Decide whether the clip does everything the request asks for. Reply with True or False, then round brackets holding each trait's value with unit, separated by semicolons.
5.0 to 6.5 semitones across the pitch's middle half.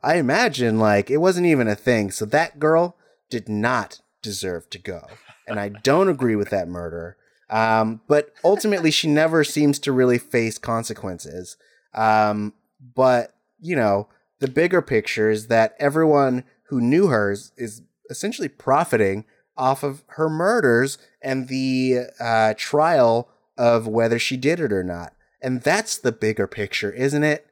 True (5.3 semitones)